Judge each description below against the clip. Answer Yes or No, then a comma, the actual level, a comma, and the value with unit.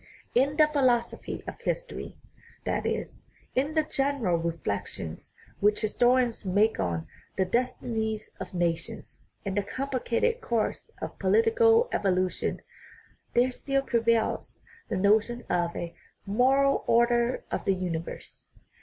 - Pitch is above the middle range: Yes, high, 230 Hz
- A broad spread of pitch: Yes, wide, 6.3 semitones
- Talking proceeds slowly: Yes, slow, 130 wpm